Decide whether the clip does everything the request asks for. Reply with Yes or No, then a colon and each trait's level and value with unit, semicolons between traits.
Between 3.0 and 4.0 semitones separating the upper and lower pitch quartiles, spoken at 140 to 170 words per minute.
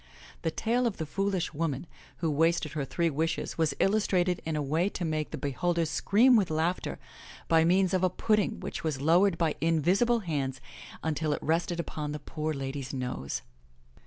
No: average, 3.3 semitones; average, 185 wpm